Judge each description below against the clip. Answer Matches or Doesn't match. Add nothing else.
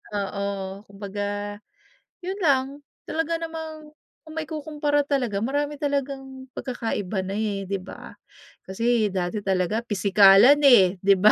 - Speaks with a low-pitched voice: Doesn't match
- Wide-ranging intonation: Matches